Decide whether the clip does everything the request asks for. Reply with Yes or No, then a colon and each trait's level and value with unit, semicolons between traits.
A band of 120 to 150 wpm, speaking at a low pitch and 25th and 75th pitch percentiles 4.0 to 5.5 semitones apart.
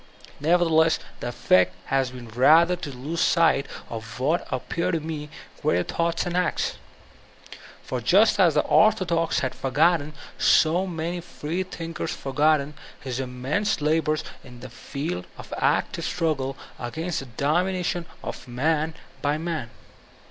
No: average, 140 wpm; medium, 155 Hz; average, 4.3 semitones